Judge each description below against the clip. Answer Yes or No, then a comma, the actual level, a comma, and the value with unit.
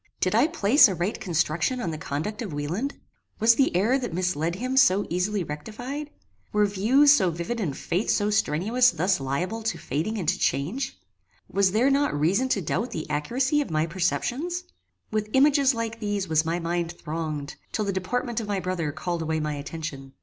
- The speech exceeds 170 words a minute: Yes, average, 190 wpm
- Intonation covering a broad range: Yes, wide, 6.4 semitones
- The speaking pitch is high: Yes, high, 195 Hz